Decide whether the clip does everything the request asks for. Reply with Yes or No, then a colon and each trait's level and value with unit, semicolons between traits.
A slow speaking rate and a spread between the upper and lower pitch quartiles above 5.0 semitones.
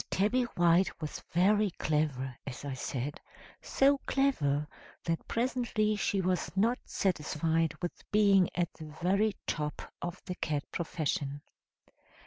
Yes: slow, 125 wpm; wide, 5.5 semitones